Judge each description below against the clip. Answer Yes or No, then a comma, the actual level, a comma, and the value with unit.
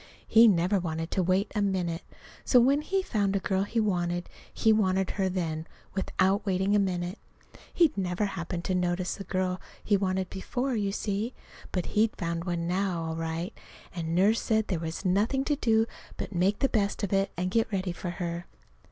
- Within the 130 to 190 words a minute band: No, average, 200 wpm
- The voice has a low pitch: No, high, 190 Hz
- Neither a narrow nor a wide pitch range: Yes, average, 3.0 semitones